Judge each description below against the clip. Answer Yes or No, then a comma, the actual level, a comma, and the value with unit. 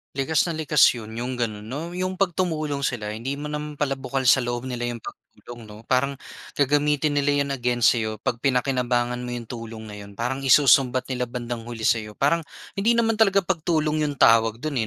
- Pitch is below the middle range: Yes, low, 130 Hz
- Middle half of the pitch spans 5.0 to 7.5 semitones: No, average, 3.9 semitones